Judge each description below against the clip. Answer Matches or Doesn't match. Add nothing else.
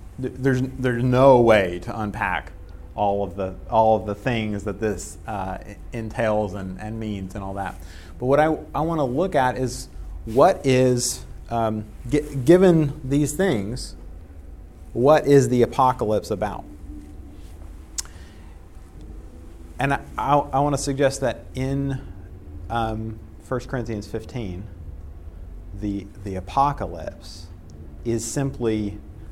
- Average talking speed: Doesn't match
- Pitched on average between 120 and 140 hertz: Doesn't match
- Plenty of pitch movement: Matches